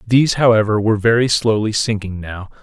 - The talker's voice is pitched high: No, low, 110 Hz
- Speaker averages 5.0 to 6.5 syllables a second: Yes, 5.9 syllables/s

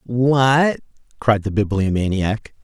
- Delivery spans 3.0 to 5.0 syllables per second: Yes, 3.4 syllables/s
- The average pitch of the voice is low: Yes, low, 115 Hz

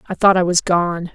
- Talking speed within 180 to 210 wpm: No, fast, 265 wpm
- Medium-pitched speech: Yes, medium, 175 Hz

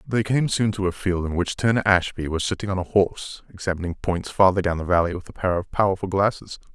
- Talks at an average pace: No, fast, 240 wpm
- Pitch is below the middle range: Yes, very low, 95 Hz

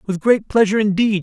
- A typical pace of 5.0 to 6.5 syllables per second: Yes, 5.7 syllables/s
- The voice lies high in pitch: Yes, high, 205 Hz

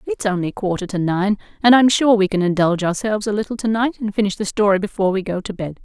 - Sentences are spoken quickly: Yes, fast, 255 wpm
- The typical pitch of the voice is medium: No, high, 205 Hz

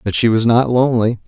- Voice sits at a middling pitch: No, low, 115 Hz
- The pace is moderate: No, fast, 235 wpm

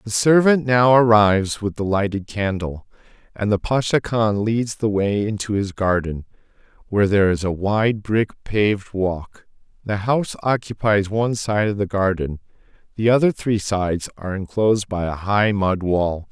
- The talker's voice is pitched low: Yes, low, 105 Hz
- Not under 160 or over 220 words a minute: Yes, average, 165 wpm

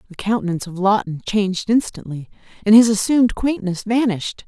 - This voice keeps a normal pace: Yes, average, 145 wpm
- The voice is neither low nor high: No, high, 210 Hz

